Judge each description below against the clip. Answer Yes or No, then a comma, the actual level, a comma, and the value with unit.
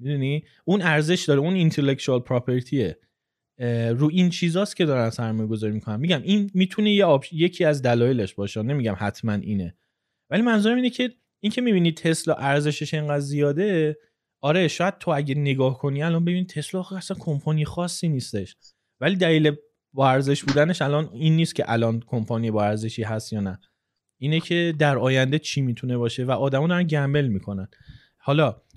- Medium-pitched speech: Yes, medium, 145 Hz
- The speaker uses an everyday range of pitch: No, wide, 5.8 semitones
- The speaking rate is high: Yes, fast, 165 wpm